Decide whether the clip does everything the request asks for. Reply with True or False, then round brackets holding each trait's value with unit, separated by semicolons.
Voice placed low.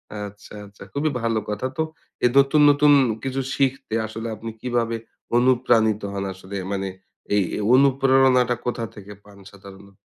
True (115 Hz)